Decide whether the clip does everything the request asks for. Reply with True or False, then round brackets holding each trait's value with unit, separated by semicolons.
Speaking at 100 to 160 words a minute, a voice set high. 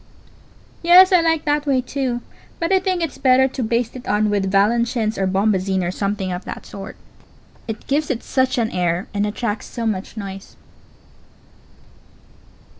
False (170 wpm; 230 Hz)